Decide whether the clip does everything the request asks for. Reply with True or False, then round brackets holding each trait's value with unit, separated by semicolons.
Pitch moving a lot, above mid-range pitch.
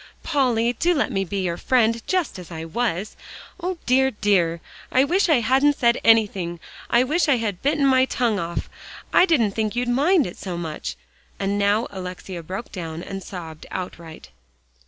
True (6.3 semitones; 220 Hz)